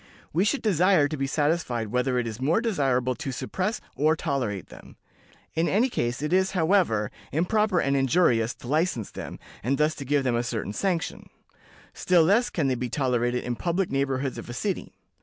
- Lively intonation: Yes, wide, 6.3 semitones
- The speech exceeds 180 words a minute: Yes, average, 190 wpm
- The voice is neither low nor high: Yes, medium, 145 Hz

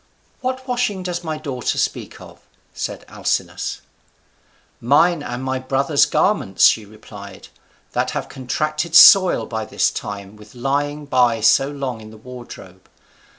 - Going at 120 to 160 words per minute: Yes, average, 140 wpm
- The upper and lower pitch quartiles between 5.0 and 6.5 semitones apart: Yes, wide, 5.4 semitones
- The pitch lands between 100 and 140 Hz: Yes, low, 135 Hz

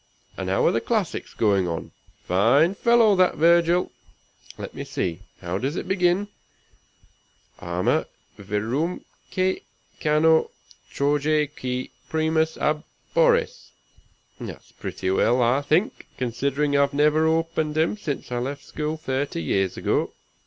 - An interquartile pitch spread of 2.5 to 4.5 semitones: No, average, 5.3 semitones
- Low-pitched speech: No, medium, 150 Hz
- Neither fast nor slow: No, slow, 125 wpm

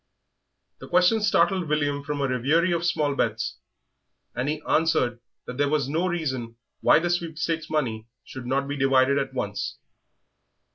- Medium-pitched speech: Yes, medium, 145 Hz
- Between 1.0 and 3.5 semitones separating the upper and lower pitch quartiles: No, average, 4.0 semitones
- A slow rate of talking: No, average, 155 wpm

